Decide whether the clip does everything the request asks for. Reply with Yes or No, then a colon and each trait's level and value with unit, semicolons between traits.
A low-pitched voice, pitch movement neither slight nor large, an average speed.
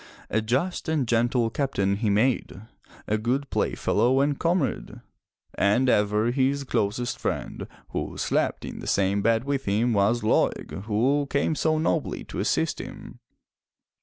Yes: low, 120 Hz; average, 4.7 semitones; average, 145 wpm